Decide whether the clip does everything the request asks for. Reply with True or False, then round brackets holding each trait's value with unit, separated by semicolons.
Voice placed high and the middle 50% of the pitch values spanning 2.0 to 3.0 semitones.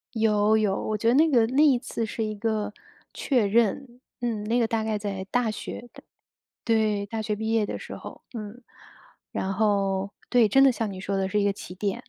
True (220 Hz; 2.4 semitones)